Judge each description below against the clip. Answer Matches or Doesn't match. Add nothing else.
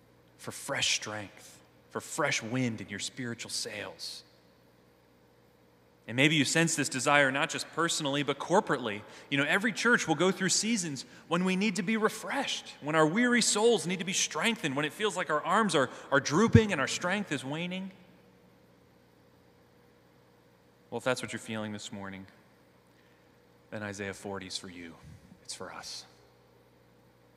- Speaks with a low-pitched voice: Matches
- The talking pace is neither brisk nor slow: Matches